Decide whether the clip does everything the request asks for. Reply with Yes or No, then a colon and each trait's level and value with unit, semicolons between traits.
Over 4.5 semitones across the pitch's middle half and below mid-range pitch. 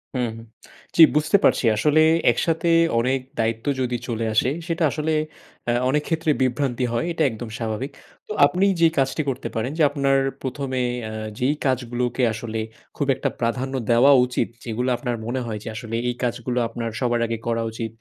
No: average, 3.1 semitones; low, 125 Hz